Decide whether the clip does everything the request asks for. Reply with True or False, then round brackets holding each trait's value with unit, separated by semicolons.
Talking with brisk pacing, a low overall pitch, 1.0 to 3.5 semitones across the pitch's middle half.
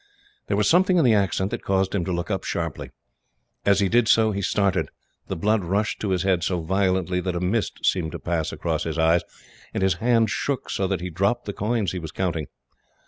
True (225 wpm; 95 Hz; 3.1 semitones)